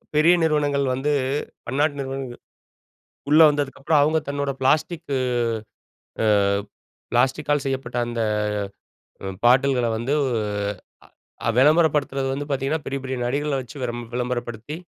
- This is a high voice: No, medium, 140 Hz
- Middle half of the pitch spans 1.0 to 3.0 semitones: Yes, narrow, 2.6 semitones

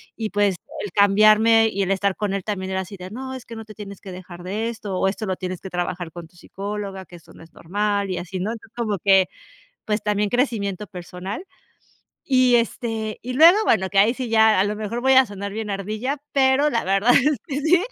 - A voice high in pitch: Yes, high, 210 Hz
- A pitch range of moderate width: Yes, average, 3.2 semitones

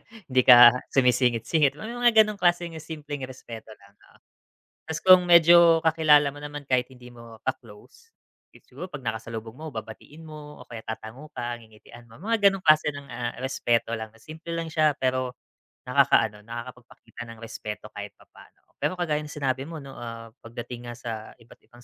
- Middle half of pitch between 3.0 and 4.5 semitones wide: No, average, 5.0 semitones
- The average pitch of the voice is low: Yes, low, 130 Hz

